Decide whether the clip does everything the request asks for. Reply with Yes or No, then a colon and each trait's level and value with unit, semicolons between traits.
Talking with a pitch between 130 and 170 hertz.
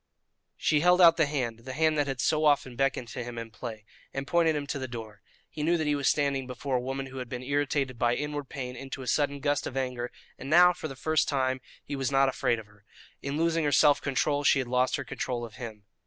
Yes: low, 135 Hz